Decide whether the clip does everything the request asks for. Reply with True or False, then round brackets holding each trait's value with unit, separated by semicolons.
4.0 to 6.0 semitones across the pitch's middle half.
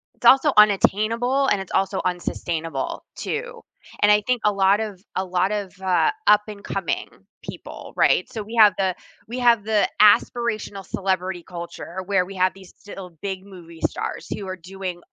False (2.5 semitones)